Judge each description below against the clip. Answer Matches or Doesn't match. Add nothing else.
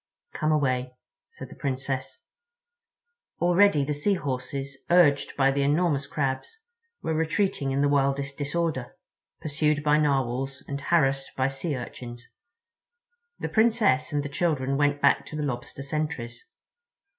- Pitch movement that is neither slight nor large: Doesn't match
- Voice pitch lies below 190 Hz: Matches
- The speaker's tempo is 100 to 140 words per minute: Matches